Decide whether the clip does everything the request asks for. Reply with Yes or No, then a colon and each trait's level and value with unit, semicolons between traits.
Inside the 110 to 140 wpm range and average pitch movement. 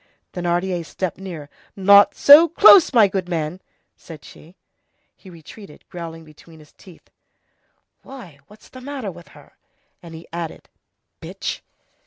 Yes: slow, 135 wpm; average, 3.7 semitones